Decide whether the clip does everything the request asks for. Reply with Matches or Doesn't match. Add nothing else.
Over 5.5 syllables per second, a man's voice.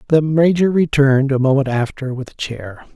Doesn't match